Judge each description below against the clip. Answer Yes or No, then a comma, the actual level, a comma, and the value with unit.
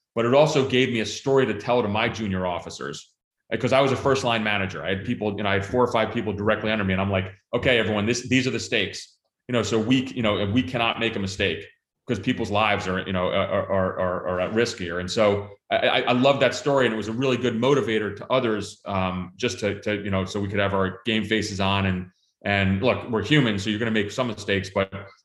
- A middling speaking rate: No, fast, 265 wpm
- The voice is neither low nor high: No, low, 110 Hz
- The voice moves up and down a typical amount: Yes, average, 3.6 semitones